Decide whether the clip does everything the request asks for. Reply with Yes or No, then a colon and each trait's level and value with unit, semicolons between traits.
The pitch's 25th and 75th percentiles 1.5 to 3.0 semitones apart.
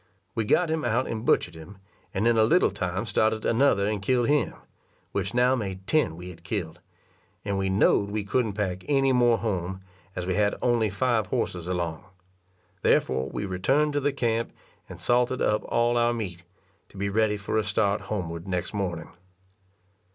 No: average, 4.1 semitones